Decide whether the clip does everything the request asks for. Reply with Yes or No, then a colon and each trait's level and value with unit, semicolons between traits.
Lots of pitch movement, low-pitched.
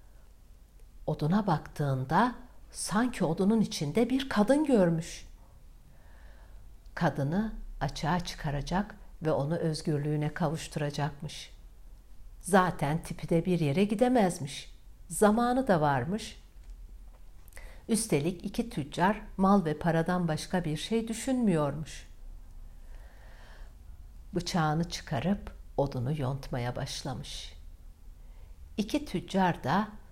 No: wide, 6.4 semitones; medium, 160 Hz